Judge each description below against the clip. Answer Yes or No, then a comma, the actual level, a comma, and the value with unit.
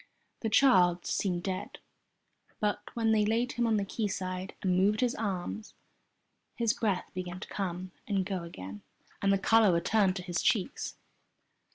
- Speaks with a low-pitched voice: No, high, 195 Hz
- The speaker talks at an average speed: Yes, average, 160 wpm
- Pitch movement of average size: Yes, average, 3.3 semitones